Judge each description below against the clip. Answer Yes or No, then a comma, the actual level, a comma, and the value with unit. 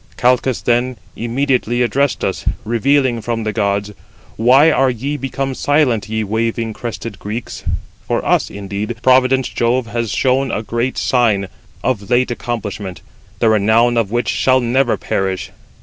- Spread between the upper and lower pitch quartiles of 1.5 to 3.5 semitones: Yes, average, 2.8 semitones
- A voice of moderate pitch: No, low, 120 Hz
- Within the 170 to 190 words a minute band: No, average, 150 wpm